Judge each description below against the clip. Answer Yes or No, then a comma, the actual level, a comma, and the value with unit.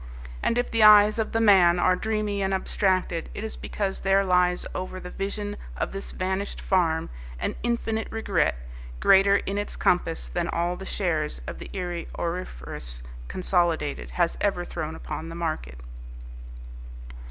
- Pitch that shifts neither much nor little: Yes, average, 3.1 semitones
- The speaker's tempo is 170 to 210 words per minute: No, average, 155 wpm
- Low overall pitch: No, medium, 185 Hz